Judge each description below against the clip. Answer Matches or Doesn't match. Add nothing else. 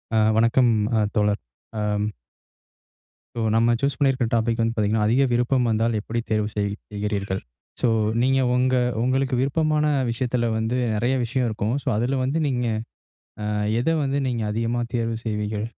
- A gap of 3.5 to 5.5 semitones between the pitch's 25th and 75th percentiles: Doesn't match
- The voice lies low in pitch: Matches